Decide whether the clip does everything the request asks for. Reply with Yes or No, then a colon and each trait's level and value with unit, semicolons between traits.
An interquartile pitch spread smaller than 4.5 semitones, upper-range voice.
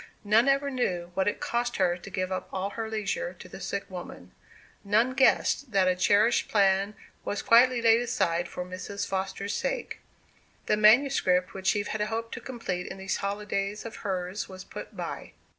Yes: average, 3.5 semitones; high, 205 Hz